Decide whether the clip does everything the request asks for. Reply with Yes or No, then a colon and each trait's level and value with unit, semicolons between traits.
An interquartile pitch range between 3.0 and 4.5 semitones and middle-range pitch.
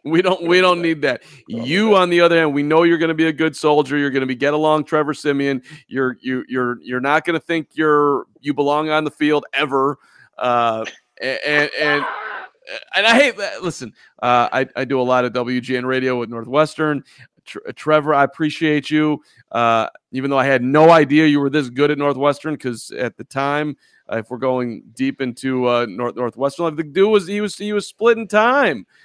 Yes: average, 3.4 semitones; medium, 145 Hz